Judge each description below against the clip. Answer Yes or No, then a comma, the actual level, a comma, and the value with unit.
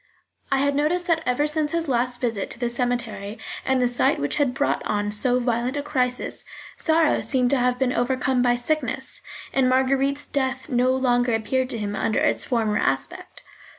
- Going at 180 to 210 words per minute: Yes, average, 185 wpm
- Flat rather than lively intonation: Yes, narrow, 2.3 semitones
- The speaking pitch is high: Yes, very high, 255 Hz